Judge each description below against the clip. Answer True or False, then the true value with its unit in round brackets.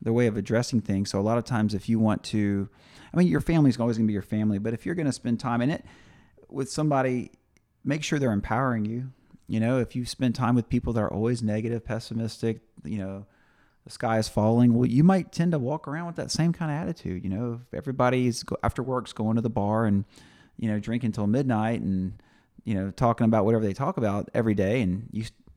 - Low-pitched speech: True (115 Hz)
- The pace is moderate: False (240 wpm)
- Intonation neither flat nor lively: True (3.1 semitones)